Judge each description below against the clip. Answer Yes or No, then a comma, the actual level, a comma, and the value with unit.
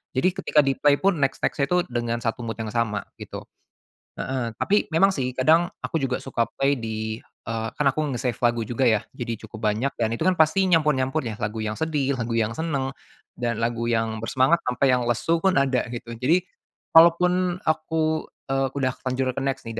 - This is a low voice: Yes, low, 130 Hz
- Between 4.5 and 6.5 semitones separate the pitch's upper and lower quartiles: Yes, average, 5.1 semitones